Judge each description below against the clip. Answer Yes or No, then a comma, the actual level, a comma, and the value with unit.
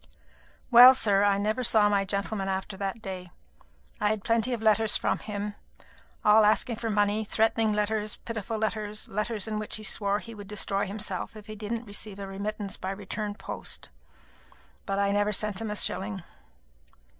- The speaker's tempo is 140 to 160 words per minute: No, average, 180 wpm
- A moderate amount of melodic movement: No, narrow, 1.5 semitones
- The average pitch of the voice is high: Yes, high, 210 Hz